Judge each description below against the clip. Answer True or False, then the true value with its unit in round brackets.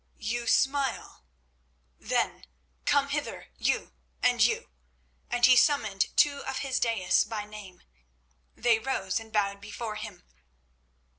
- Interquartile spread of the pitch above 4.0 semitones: False (3.7 semitones)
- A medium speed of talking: False (120 wpm)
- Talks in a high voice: True (220 Hz)